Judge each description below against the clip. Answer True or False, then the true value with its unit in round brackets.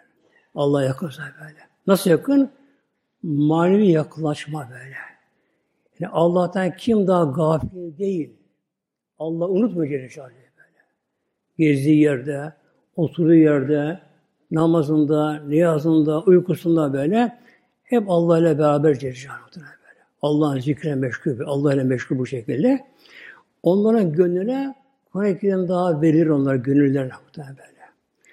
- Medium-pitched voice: True (160 Hz)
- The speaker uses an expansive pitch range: False (3.9 semitones)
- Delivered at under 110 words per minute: True (100 wpm)